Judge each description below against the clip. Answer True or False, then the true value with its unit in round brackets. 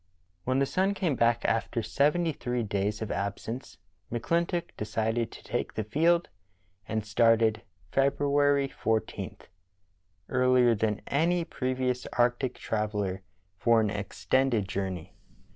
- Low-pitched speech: True (120 Hz)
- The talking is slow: True (120 wpm)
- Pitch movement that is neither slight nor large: True (4.3 semitones)